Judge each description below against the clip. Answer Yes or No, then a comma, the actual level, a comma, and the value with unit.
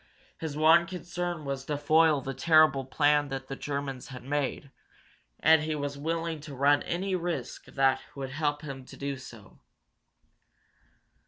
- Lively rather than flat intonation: No, average, 2.8 semitones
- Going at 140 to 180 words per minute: Yes, average, 155 wpm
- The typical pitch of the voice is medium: Yes, medium, 145 Hz